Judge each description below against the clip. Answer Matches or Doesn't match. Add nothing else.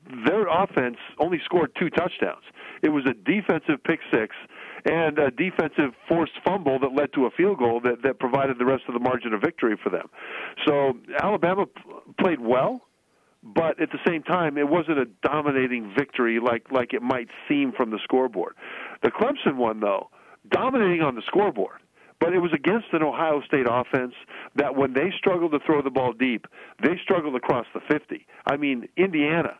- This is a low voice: Doesn't match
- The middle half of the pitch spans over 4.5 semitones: Matches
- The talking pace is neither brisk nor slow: Matches